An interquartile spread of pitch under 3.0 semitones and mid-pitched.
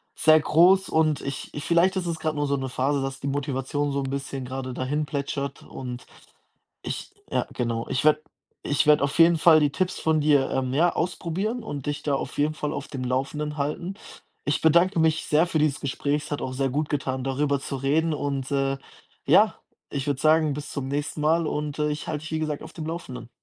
Yes: narrow, 2.4 semitones; medium, 145 Hz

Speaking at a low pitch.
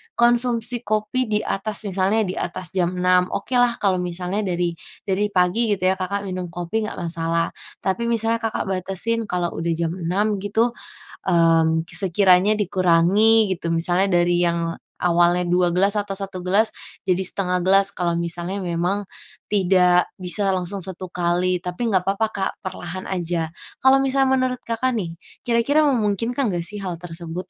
No: medium, 185 Hz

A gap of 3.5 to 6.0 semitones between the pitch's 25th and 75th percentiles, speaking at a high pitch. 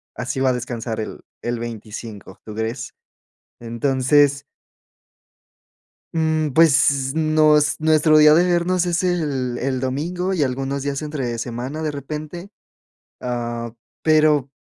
No: average, 4.1 semitones; medium, 140 Hz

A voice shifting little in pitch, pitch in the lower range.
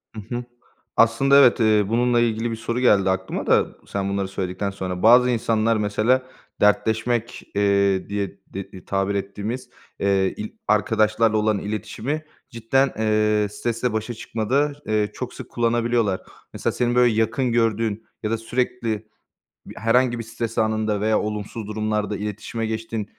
Yes: narrow, 2.3 semitones; low, 110 Hz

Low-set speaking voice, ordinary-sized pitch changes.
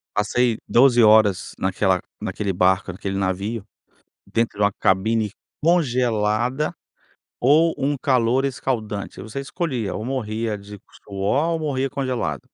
Yes: low, 115 Hz; average, 4.4 semitones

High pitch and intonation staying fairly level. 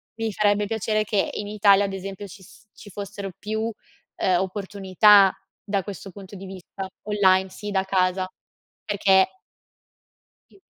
Yes: high, 200 Hz; narrow, 1.5 semitones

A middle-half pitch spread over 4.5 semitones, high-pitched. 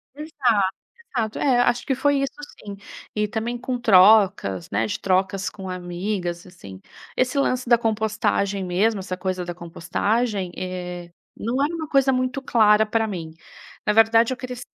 Yes: average, 5.0 semitones; high, 215 Hz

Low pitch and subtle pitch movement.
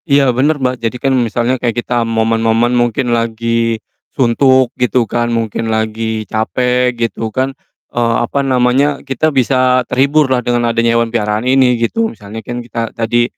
Yes: low, 120 Hz; narrow, 2.0 semitones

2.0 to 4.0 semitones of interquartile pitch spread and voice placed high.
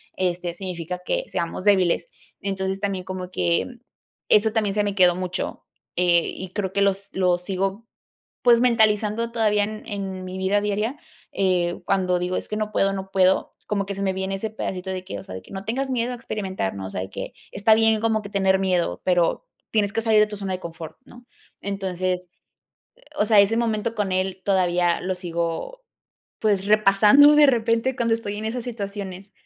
Yes: average, 2.8 semitones; high, 195 Hz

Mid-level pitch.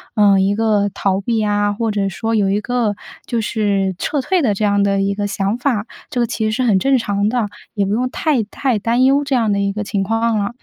No: high, 210 Hz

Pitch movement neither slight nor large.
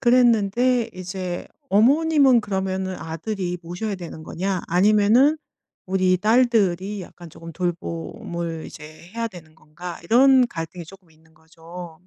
Yes: average, 4.7 semitones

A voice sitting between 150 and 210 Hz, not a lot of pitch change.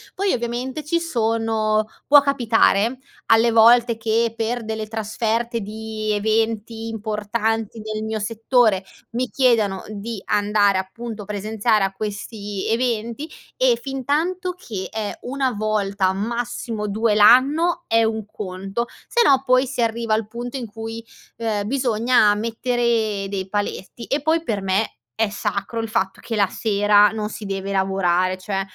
No: high, 220 Hz; narrow, 2.3 semitones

